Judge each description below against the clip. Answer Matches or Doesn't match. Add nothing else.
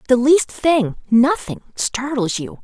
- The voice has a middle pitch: Doesn't match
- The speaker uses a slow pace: Matches